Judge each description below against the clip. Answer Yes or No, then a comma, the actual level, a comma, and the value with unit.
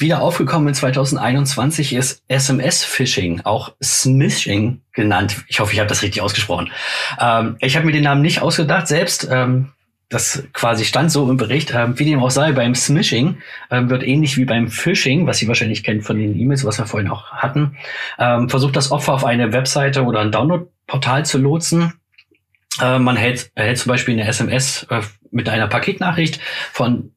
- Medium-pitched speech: No, low, 130 Hz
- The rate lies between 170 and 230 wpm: Yes, average, 185 wpm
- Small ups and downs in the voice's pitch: No, average, 3.4 semitones